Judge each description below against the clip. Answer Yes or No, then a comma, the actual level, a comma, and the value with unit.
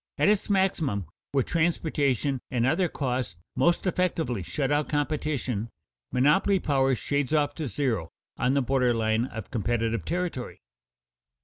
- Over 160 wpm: No, slow, 135 wpm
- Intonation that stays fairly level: No, average, 4.6 semitones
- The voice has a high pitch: No, low, 135 Hz